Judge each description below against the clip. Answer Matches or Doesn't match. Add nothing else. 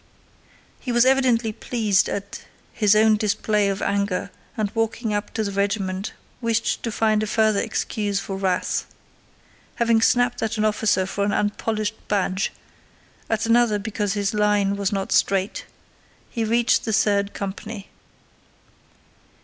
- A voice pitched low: Doesn't match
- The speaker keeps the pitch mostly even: Matches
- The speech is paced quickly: Doesn't match